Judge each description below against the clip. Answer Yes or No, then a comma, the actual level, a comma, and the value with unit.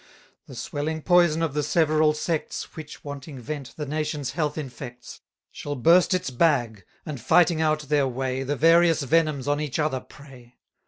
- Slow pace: No, average, 165 wpm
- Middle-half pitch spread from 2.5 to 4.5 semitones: Yes, average, 2.9 semitones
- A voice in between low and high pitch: Yes, medium, 150 Hz